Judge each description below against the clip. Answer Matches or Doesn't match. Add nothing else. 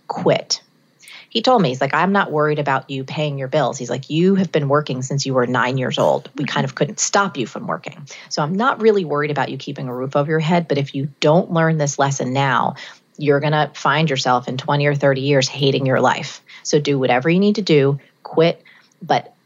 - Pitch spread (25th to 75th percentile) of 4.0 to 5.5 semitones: Doesn't match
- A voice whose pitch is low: Doesn't match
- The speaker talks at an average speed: Doesn't match